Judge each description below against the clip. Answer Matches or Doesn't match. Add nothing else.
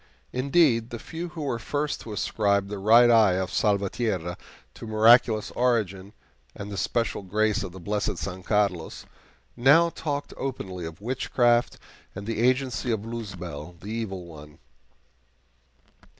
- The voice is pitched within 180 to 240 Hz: Doesn't match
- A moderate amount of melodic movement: Matches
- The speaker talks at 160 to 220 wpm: Doesn't match